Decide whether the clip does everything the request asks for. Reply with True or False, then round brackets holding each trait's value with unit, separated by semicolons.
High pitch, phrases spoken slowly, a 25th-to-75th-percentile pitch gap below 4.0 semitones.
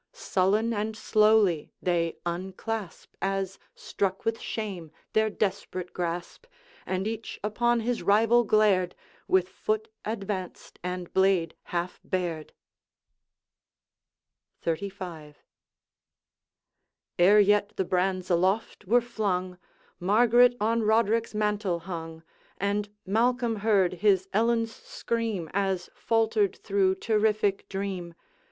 True (200 Hz; 105 wpm; 3.1 semitones)